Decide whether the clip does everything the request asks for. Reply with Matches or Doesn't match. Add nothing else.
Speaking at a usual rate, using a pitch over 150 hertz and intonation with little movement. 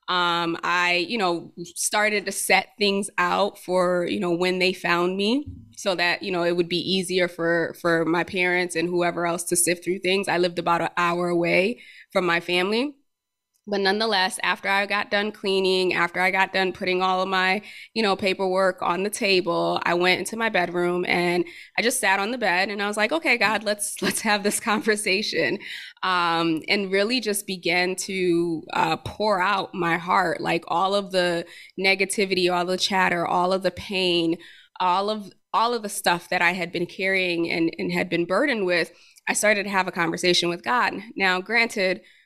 Matches